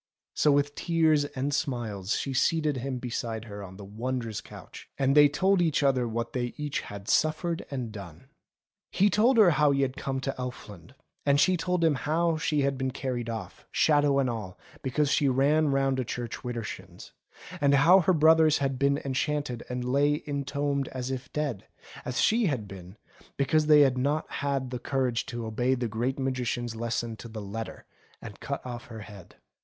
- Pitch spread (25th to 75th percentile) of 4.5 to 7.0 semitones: No, average, 3.7 semitones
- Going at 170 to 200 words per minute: Yes, average, 190 wpm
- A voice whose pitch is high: No, low, 135 Hz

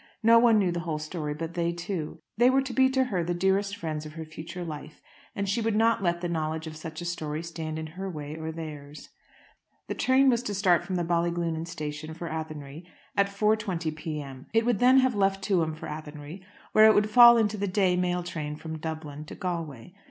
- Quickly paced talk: Yes, fast, 220 wpm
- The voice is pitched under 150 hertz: No, medium, 170 Hz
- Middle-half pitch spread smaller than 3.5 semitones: No, average, 4.3 semitones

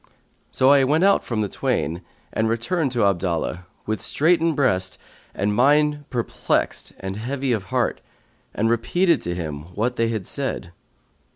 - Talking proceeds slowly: No, average, 155 wpm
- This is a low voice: Yes, low, 115 Hz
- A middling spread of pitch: No, wide, 6.6 semitones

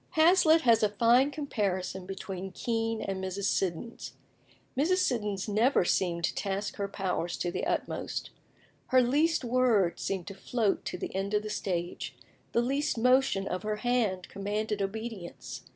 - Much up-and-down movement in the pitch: No, average, 4.3 semitones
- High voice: Yes, high, 210 Hz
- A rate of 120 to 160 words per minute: Yes, average, 155 wpm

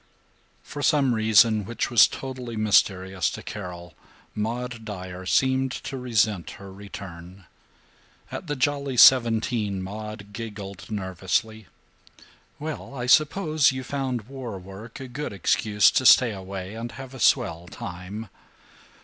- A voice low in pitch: Yes, low, 110 Hz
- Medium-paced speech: No, slow, 130 wpm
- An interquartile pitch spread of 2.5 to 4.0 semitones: No, average, 4.8 semitones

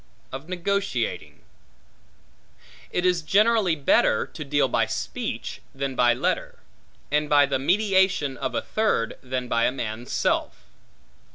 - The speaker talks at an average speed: No, slow, 130 wpm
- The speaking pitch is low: No, medium, 145 Hz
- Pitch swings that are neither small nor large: No, wide, 6.4 semitones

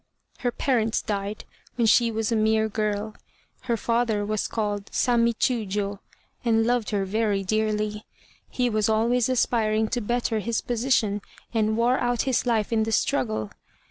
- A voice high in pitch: Yes, high, 220 Hz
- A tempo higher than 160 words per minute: No, average, 155 wpm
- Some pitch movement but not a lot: No, narrow, 2.0 semitones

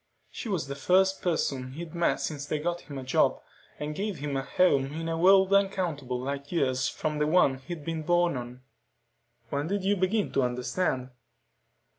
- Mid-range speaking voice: Yes, medium, 155 Hz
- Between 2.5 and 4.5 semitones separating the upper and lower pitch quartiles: No, average, 5.0 semitones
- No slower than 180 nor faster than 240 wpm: Yes, average, 185 wpm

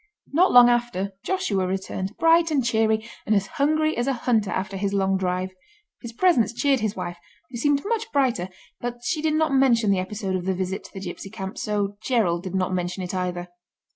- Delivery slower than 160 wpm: No, fast, 205 wpm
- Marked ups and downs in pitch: Yes, wide, 5.7 semitones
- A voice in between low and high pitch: No, high, 215 Hz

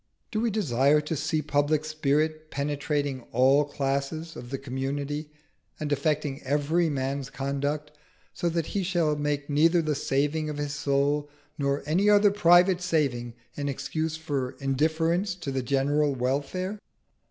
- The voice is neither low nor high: Yes, medium, 145 Hz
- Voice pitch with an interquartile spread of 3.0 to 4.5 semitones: No, narrow, 2.5 semitones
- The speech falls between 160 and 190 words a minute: No, average, 145 wpm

